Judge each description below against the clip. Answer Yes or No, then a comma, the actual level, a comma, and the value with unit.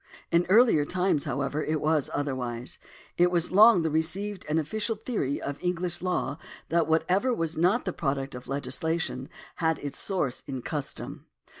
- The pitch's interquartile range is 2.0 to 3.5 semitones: No, average, 4.3 semitones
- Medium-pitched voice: Yes, medium, 160 Hz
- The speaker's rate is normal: Yes, average, 160 wpm